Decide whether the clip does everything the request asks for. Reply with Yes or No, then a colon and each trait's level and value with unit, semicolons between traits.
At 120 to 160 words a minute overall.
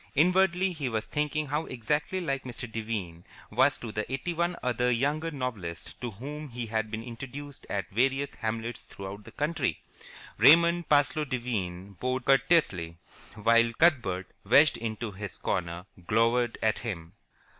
Yes: average, 145 wpm